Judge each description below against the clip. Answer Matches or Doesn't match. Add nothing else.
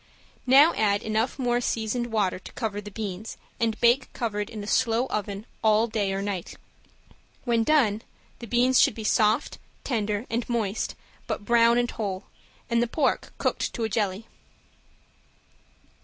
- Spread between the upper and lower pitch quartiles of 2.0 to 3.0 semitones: Matches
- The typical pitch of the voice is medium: Doesn't match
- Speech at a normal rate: Matches